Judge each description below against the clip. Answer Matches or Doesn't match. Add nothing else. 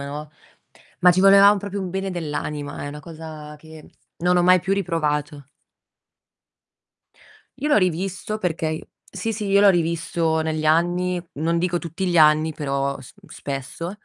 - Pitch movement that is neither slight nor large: Matches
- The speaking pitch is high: Doesn't match